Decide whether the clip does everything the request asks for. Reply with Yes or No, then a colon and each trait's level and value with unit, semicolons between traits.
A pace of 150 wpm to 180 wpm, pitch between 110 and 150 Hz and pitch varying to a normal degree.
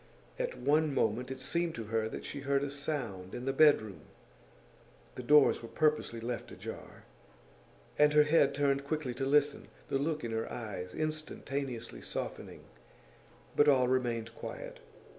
Yes: average, 155 wpm; low, 135 Hz; average, 4.2 semitones